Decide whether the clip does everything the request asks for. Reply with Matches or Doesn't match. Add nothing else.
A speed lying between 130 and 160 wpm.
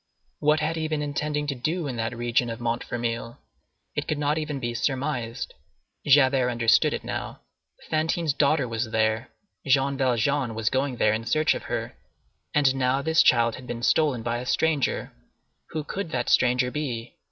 Doesn't match